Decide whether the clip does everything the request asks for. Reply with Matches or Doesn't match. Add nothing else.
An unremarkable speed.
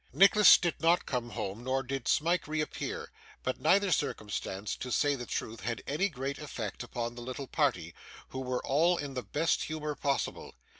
Matches